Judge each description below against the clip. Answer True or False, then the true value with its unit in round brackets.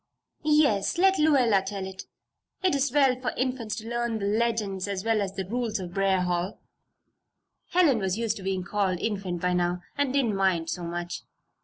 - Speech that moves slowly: False (185 wpm)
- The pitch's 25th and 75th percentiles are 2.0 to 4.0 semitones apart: False (4.6 semitones)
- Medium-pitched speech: False (205 Hz)